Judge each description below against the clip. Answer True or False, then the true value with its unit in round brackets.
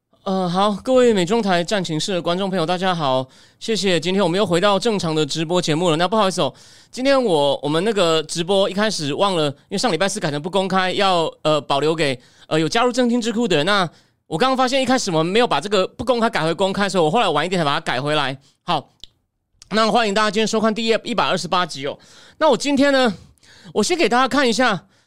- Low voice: False (185 Hz)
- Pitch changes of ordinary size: False (6.1 semitones)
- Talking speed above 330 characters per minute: True (355 characters per minute)